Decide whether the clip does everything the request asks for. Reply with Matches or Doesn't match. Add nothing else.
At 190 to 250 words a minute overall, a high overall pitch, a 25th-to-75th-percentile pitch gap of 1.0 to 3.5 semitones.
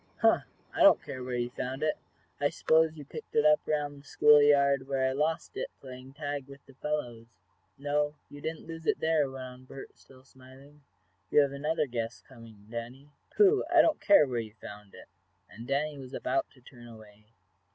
Doesn't match